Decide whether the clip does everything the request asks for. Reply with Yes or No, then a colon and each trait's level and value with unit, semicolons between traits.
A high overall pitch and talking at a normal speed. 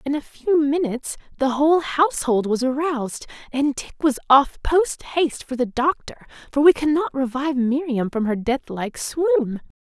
Yes: very high, 280 Hz; average, 170 wpm